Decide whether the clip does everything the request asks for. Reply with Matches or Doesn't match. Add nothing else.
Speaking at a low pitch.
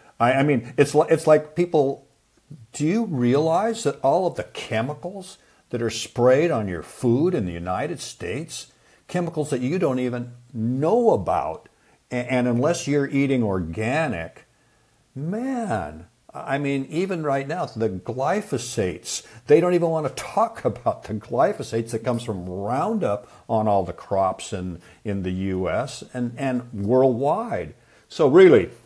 Matches